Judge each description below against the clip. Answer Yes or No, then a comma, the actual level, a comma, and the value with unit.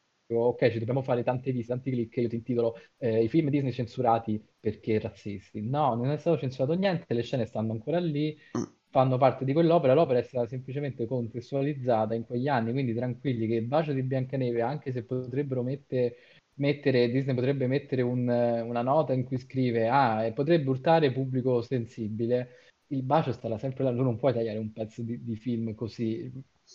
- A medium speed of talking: No, fast, 185 wpm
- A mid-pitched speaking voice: No, low, 125 Hz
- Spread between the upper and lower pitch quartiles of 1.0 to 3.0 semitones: Yes, average, 2.7 semitones